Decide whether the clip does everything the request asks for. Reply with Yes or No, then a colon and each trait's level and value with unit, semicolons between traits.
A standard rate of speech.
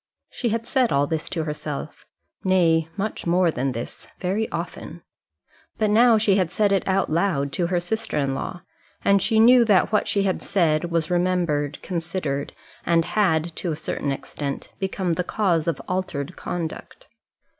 Yes: average, 170 wpm